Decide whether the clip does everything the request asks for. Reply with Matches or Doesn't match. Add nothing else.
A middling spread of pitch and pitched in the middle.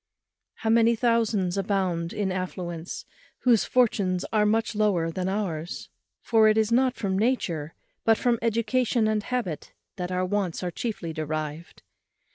Doesn't match